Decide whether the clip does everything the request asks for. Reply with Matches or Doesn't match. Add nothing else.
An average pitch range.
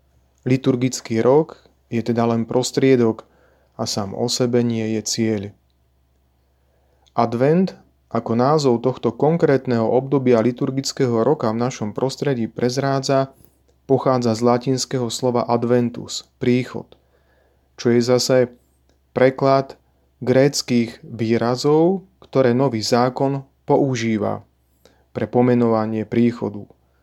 Matches